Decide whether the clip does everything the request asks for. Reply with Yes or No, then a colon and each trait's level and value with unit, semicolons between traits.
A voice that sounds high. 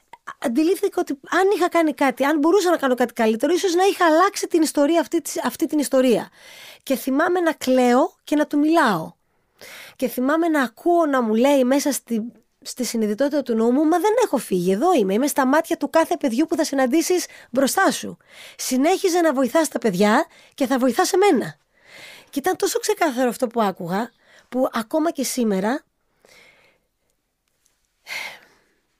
Yes: very high, 290 Hz